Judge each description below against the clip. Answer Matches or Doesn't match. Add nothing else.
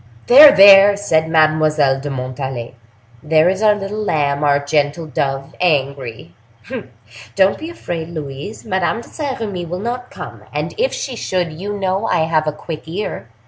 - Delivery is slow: Doesn't match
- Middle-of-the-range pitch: Matches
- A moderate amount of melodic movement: Doesn't match